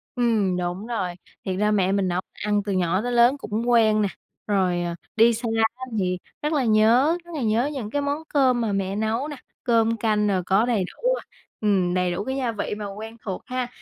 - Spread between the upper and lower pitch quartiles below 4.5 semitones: Yes, average, 3.9 semitones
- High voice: Yes, high, 215 Hz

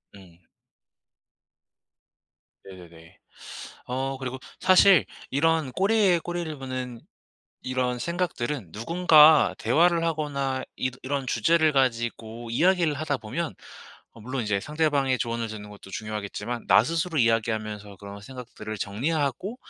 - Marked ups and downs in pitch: Yes, wide, 6.3 semitones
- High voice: No, low, 130 Hz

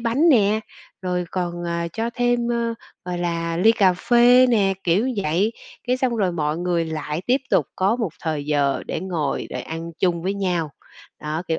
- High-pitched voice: No, medium, 180 Hz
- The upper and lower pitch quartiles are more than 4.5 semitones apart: Yes, wide, 5.5 semitones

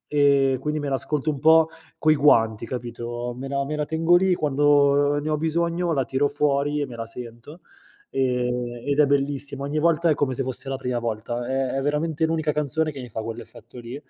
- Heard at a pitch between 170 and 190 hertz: No, medium, 140 Hz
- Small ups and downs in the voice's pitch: No, average, 3.3 semitones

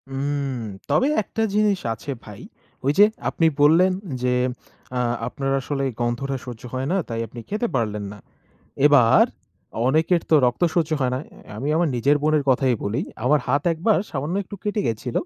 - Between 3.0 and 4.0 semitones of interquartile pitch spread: No, average, 4.9 semitones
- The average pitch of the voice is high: No, medium, 140 Hz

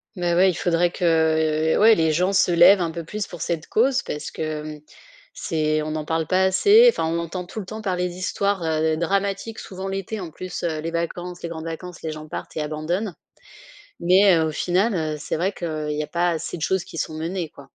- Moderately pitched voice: Yes, medium, 170 Hz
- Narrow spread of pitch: No, average, 3.0 semitones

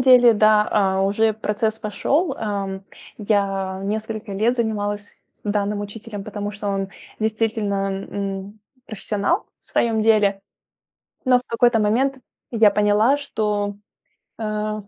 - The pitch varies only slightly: Yes, narrow, 1.7 semitones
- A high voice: Yes, high, 210 Hz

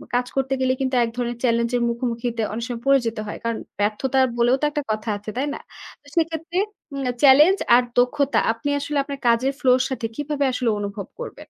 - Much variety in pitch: No, average, 3.2 semitones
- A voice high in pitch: Yes, very high, 255 Hz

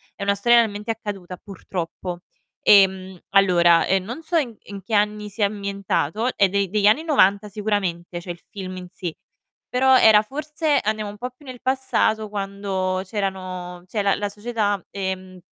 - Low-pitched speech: No, high, 200 Hz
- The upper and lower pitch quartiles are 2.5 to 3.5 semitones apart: Yes, average, 2.8 semitones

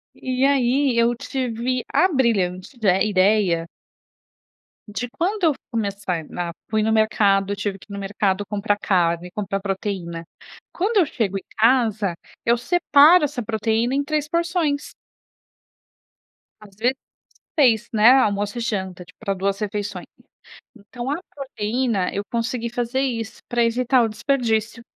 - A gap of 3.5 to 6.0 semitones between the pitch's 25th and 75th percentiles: Yes, average, 4.3 semitones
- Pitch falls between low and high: No, high, 225 Hz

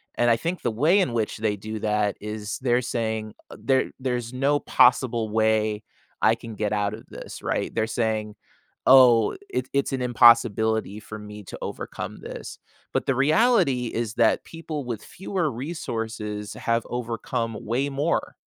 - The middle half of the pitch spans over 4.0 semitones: No, average, 3.4 semitones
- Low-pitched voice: Yes, low, 115 Hz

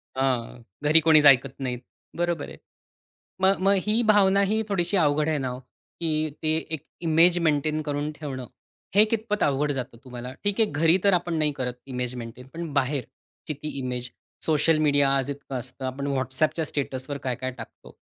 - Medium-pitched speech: Yes, medium, 145 Hz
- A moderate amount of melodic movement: Yes, average, 4.1 semitones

